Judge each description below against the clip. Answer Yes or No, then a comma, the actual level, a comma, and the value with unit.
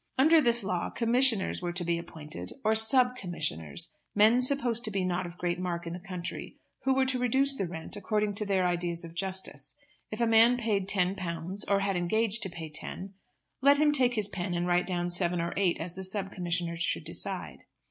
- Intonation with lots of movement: No, average, 4.5 semitones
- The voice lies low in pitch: No, high, 190 Hz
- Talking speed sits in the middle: No, fast, 210 wpm